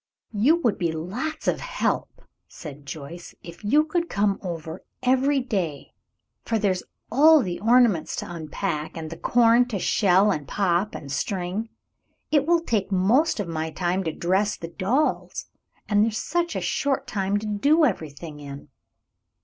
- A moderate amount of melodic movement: No, wide, 6.6 semitones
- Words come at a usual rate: Yes, average, 160 wpm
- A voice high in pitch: Yes, high, 200 Hz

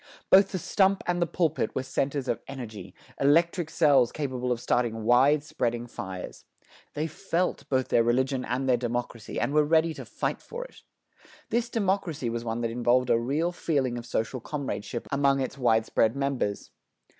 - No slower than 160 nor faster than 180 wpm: Yes, average, 170 wpm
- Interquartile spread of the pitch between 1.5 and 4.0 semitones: No, average, 4.7 semitones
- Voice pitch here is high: No, low, 130 Hz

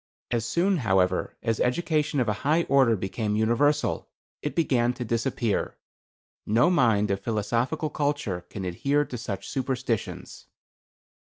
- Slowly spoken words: Yes, slow, 130 wpm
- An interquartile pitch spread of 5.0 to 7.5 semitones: Yes, average, 5.3 semitones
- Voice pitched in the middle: No, low, 120 Hz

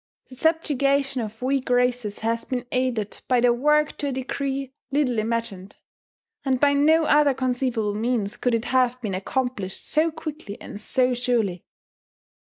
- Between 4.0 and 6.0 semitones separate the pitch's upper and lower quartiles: No, average, 3.2 semitones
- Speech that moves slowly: No, average, 155 wpm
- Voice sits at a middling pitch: No, very high, 250 Hz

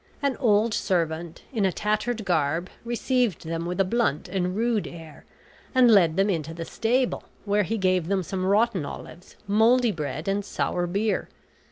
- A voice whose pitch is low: No, high, 195 Hz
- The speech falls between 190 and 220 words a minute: No, average, 170 wpm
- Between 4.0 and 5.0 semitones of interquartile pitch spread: Yes, average, 4.6 semitones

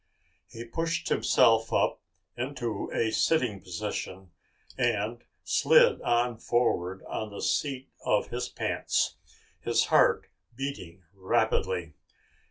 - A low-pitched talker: Yes, low, 115 Hz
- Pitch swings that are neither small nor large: Yes, average, 4.5 semitones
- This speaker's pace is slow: Yes, slow, 105 wpm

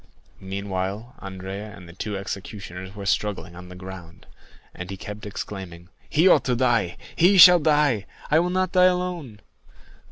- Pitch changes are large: Yes, wide, 7.8 semitones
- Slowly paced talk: No, average, 150 wpm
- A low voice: Yes, low, 105 Hz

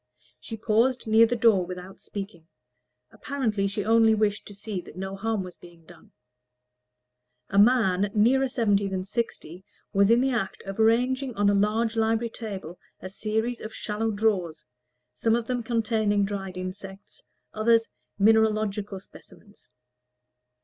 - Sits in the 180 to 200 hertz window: No, high, 215 Hz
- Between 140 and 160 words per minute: Yes, average, 145 wpm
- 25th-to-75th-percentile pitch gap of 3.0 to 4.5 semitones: No, narrow, 2.6 semitones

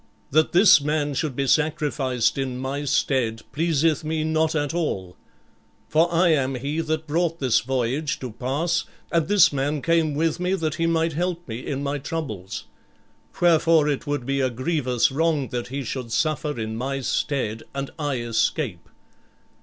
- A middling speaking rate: Yes, average, 170 wpm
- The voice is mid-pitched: Yes, medium, 145 Hz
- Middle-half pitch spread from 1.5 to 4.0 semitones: Yes, average, 3.7 semitones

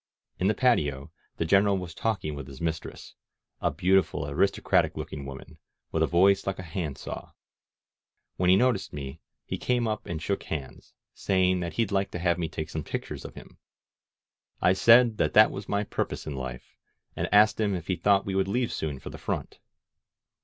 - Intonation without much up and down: No, average, 4.4 semitones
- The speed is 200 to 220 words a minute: Yes, fast, 205 wpm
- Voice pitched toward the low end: Yes, very low, 90 Hz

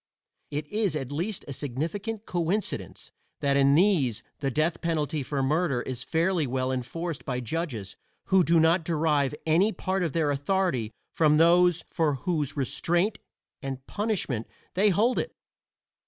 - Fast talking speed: No, average, 150 wpm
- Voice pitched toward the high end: No, medium, 160 Hz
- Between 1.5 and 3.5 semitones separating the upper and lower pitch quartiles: No, average, 4.5 semitones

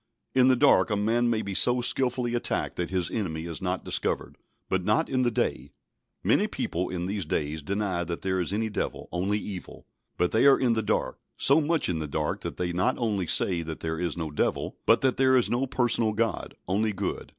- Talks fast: Yes, fast, 220 wpm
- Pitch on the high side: No, low, 105 Hz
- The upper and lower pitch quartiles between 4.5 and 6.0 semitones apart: Yes, wide, 5.5 semitones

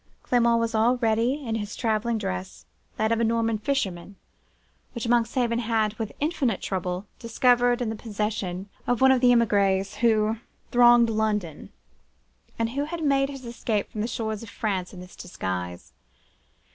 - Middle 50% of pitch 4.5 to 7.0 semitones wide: No, narrow, 2.6 semitones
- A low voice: No, high, 225 Hz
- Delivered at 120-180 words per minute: Yes, average, 160 wpm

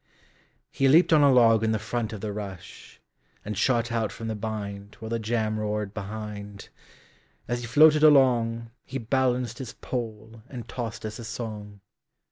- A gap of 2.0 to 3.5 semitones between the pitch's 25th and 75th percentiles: Yes, narrow, 2.4 semitones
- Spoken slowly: No, average, 145 wpm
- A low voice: Yes, low, 115 Hz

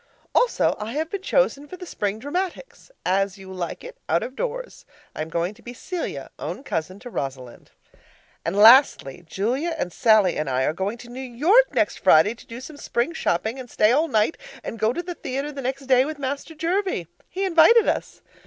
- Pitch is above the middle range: Yes, very high, 250 Hz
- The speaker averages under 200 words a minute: No, fast, 205 wpm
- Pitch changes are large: Yes, wide, 8.5 semitones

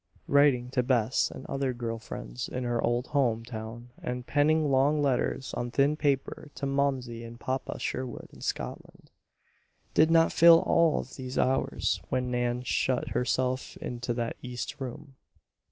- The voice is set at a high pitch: No, low, 130 Hz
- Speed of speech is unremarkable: Yes, average, 155 wpm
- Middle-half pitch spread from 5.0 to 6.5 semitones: No, narrow, 2.5 semitones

